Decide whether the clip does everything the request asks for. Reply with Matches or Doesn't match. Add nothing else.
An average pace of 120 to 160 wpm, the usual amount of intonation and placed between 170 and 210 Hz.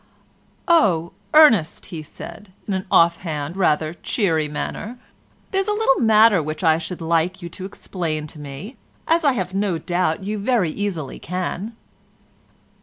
Matches